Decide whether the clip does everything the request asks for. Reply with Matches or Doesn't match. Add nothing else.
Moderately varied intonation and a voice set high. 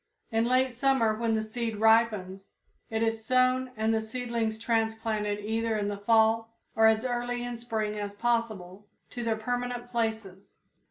Doesn't match